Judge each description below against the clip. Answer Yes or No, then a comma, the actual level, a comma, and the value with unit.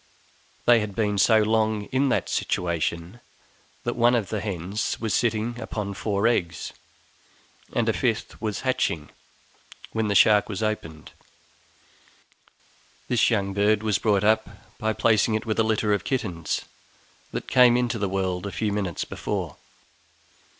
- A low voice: Yes, low, 105 Hz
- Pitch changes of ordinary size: No, narrow, 2.3 semitones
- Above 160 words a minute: No, average, 150 wpm